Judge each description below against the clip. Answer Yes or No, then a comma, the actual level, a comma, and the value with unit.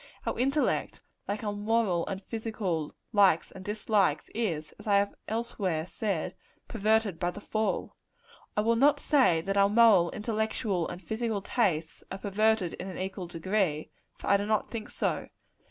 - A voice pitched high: Yes, high, 205 Hz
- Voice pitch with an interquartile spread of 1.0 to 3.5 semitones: Yes, average, 3.2 semitones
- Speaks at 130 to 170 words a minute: Yes, average, 165 wpm